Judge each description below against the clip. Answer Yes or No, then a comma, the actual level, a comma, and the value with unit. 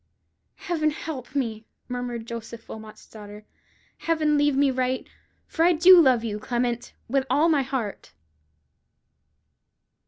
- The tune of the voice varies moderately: Yes, average, 4.4 semitones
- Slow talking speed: Yes, slow, 125 wpm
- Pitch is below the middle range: No, very high, 255 Hz